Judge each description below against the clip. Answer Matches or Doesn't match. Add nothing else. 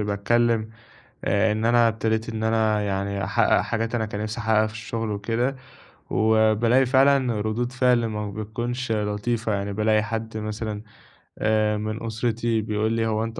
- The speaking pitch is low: Matches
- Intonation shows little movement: Matches